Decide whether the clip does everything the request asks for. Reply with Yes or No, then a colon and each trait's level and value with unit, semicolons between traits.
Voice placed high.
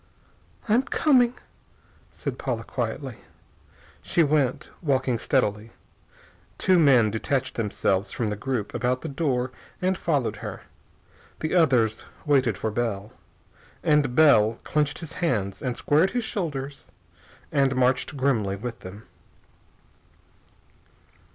No: low, 130 Hz